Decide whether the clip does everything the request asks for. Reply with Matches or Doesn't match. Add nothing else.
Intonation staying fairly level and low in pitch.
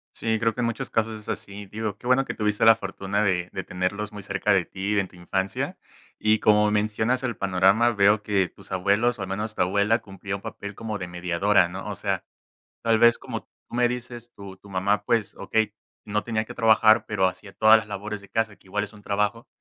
Matches